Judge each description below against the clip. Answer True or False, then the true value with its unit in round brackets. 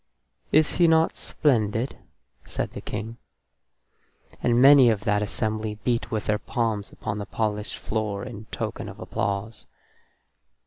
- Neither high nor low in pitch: False (110 Hz)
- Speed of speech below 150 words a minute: True (135 wpm)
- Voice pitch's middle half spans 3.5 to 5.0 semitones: False (2.6 semitones)